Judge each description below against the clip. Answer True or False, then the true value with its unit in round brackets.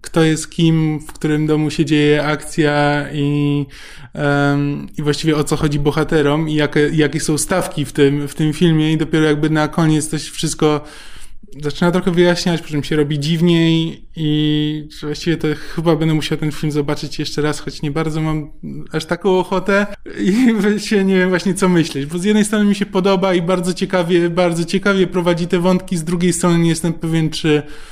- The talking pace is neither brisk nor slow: False (190 wpm)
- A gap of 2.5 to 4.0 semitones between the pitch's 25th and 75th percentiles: True (2.9 semitones)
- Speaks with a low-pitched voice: False (155 Hz)